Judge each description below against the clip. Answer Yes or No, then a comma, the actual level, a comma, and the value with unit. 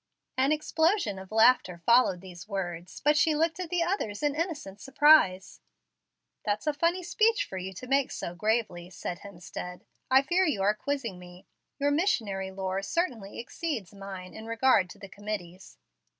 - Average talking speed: Yes, average, 165 wpm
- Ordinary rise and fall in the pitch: No, wide, 7.8 semitones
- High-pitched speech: Yes, high, 220 Hz